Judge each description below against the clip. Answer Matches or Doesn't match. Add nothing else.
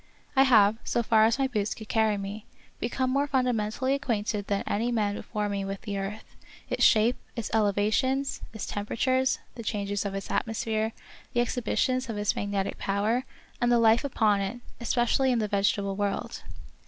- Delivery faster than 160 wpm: Matches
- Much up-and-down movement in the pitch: Doesn't match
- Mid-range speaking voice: Doesn't match